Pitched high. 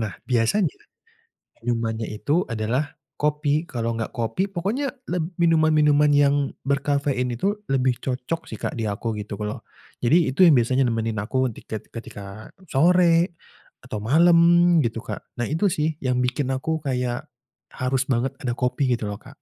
No: low, 130 Hz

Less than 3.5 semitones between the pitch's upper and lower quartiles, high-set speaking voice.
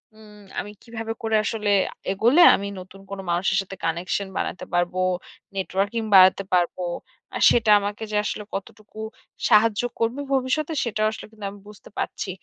Yes: narrow, 2.6 semitones; high, 210 Hz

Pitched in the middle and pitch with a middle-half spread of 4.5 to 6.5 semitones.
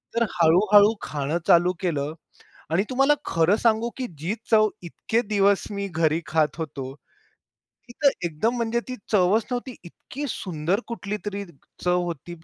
No: high, 195 Hz; average, 5.1 semitones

